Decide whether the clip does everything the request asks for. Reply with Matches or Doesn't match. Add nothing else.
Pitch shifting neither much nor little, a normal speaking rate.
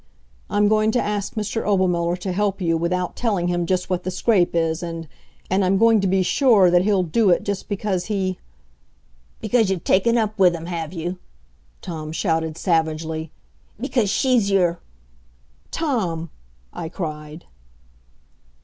Matches